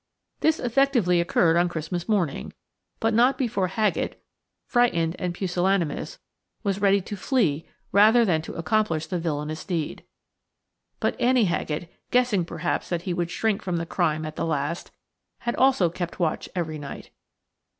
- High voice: No, medium, 180 Hz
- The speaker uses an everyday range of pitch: Yes, average, 4.7 semitones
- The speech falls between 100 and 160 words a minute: Yes, average, 150 wpm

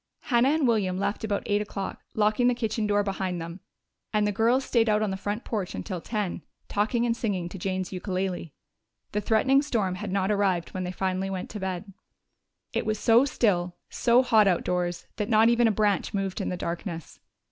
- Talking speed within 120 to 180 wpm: No, average, 200 wpm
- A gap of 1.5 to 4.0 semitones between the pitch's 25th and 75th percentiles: Yes, average, 3.1 semitones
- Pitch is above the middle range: Yes, high, 205 Hz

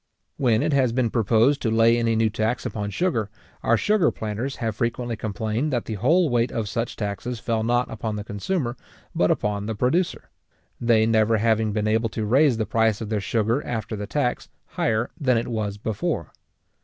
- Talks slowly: No, average, 190 wpm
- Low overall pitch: Yes, low, 115 Hz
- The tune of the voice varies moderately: No, narrow, 2.1 semitones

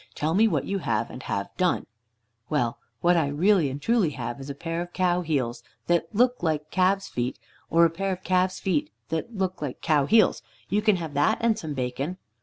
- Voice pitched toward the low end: No, medium, 170 Hz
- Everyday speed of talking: No, fast, 210 wpm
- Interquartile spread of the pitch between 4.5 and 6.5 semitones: Yes, average, 4.9 semitones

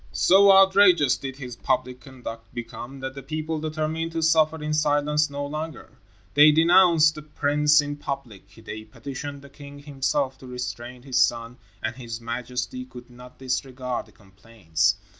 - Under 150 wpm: No, average, 160 wpm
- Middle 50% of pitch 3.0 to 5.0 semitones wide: Yes, average, 3.6 semitones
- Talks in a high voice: No, low, 135 Hz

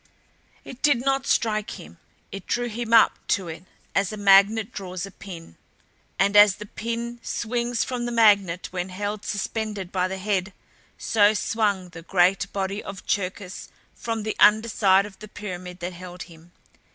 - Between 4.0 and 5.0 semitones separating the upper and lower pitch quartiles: No, average, 3.1 semitones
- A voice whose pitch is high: Yes, high, 200 Hz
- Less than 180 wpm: Yes, average, 170 wpm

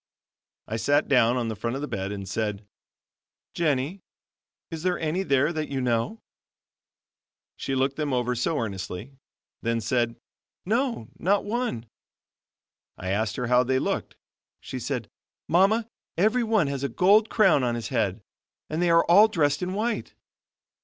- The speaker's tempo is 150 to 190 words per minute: Yes, average, 160 wpm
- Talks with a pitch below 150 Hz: Yes, medium, 140 Hz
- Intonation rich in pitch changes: Yes, wide, 7.6 semitones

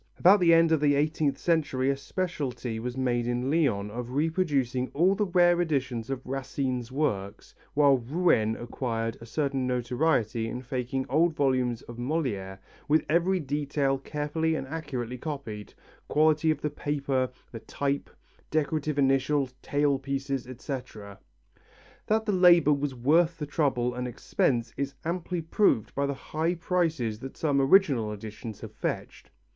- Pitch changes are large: No, average, 4.2 semitones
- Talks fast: No, average, 150 wpm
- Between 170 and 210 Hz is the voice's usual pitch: No, medium, 140 Hz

